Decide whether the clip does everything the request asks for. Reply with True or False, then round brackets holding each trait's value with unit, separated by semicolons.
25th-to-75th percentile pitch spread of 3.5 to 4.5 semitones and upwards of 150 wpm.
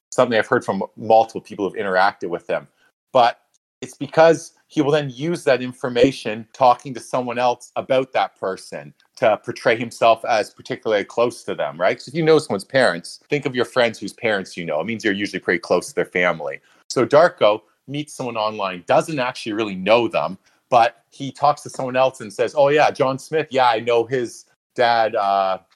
True (3.9 semitones; 200 wpm)